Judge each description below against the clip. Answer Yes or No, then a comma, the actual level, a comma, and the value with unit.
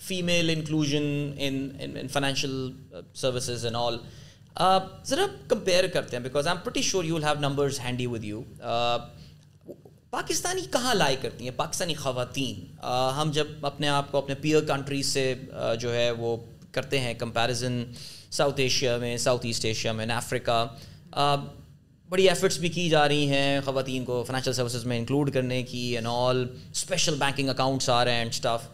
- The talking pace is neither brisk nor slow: Yes, average, 165 wpm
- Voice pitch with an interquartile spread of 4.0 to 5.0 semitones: No, average, 3.4 semitones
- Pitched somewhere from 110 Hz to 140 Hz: Yes, low, 135 Hz